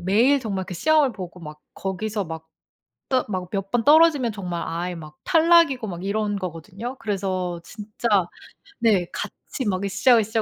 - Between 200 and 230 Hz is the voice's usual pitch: Yes, high, 205 Hz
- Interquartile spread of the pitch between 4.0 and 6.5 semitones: Yes, average, 4.9 semitones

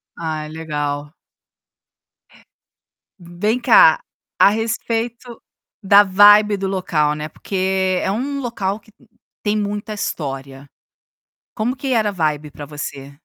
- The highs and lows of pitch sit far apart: Yes, wide, 6.1 semitones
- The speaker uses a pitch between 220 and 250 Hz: No, high, 195 Hz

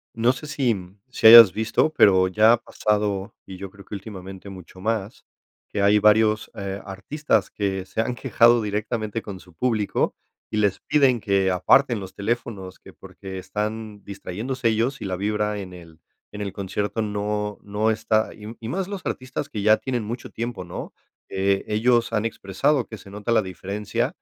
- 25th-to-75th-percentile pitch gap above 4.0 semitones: No, average, 2.7 semitones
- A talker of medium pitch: No, low, 105 Hz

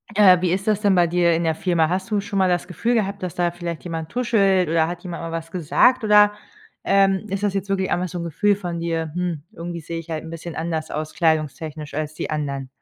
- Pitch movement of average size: Yes, average, 3.1 semitones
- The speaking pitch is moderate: Yes, medium, 175 Hz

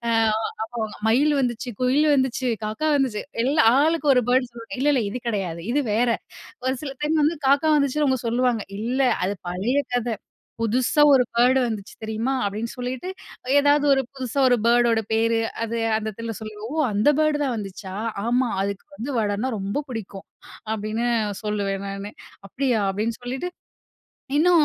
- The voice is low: No, high, 240 Hz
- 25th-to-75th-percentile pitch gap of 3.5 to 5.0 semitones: Yes, average, 3.9 semitones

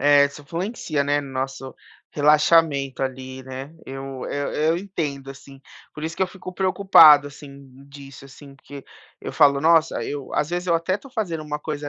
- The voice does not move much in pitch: No, average, 3.1 semitones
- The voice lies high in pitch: No, medium, 145 Hz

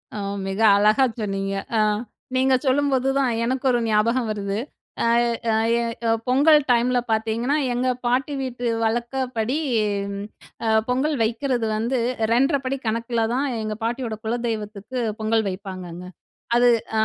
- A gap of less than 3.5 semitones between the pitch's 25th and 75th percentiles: Yes, average, 3.1 semitones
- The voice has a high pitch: Yes, high, 240 Hz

